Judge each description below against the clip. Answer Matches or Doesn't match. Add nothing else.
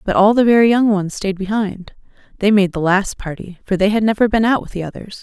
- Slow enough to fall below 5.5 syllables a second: Doesn't match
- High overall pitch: Matches